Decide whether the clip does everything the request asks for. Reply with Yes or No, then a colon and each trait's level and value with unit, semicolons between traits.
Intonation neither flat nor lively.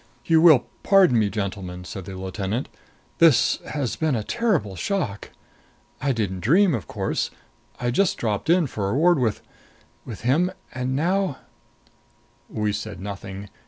No: wide, 8.3 semitones